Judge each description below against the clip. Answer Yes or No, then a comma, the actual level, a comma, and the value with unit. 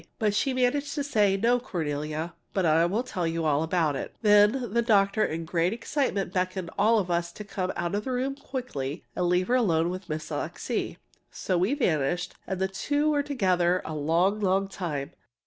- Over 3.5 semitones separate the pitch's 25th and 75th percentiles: Yes, average, 5.3 semitones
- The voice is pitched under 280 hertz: Yes, high, 190 Hz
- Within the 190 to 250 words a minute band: Yes, average, 195 wpm